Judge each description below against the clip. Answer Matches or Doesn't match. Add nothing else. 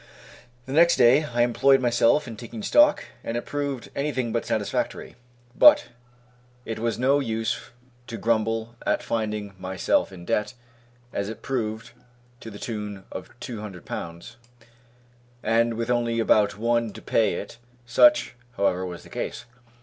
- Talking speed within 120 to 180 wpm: Matches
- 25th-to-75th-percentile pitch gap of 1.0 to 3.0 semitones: Matches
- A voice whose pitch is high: Doesn't match